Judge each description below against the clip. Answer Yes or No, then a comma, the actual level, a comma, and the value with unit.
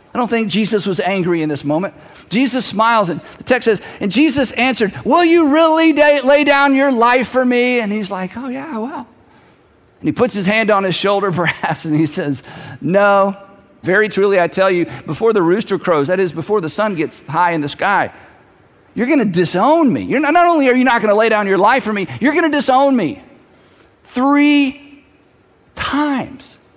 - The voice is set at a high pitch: Yes, high, 220 Hz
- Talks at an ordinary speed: No, fast, 210 wpm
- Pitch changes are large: Yes, wide, 6.4 semitones